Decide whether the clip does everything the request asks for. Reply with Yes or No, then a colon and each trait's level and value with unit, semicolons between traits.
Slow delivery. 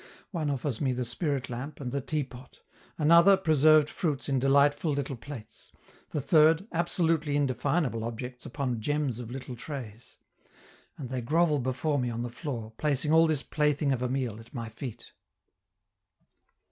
No: average, 160 wpm